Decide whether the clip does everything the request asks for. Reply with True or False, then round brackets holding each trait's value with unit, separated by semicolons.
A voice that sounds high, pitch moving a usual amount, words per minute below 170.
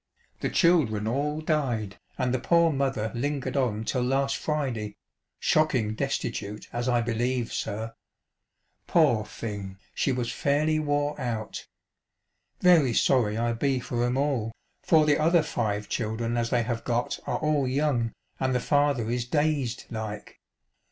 False (125 Hz; 4.2 semitones; 145 wpm)